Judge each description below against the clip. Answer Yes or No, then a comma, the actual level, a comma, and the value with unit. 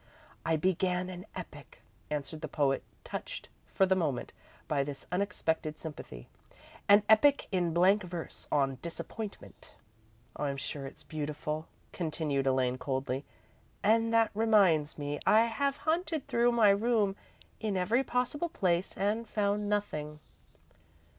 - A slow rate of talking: Yes, slow, 130 wpm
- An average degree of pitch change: No, wide, 6.3 semitones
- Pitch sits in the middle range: Yes, medium, 180 Hz